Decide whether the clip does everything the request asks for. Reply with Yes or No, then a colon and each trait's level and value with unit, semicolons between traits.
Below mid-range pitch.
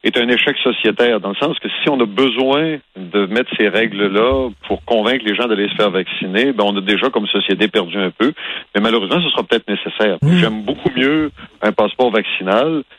Yes: low, 115 Hz